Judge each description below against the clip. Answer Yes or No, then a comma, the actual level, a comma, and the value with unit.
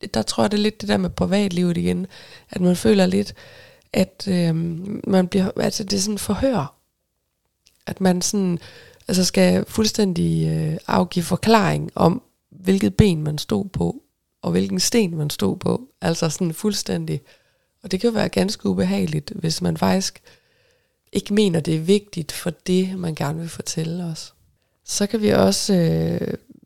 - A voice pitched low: No, medium, 180 Hz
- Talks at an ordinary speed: Yes, average, 170 wpm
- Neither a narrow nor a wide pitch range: Yes, average, 4.0 semitones